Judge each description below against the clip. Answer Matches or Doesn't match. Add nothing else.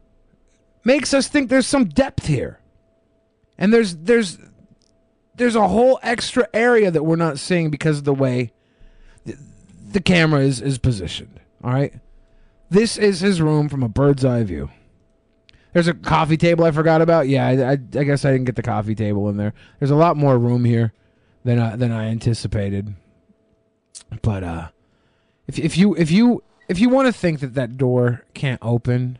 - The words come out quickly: Doesn't match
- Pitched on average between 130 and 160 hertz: Matches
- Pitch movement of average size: Doesn't match